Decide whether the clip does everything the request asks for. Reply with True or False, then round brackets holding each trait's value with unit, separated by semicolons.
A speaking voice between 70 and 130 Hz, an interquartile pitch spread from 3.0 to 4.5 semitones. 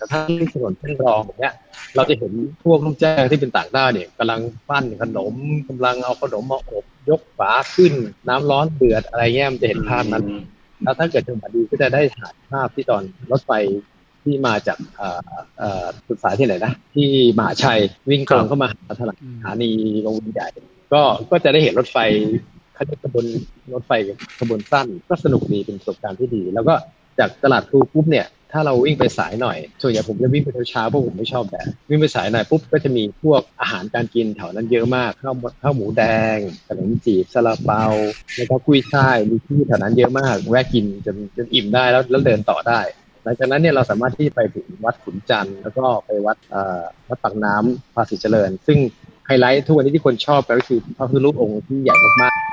True (125 Hz; 4.1 semitones)